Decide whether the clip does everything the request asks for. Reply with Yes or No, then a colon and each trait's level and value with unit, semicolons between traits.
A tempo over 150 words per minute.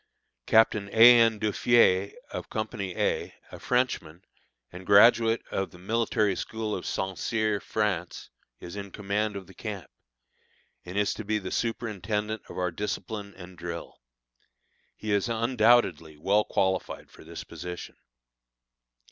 No: average, 140 wpm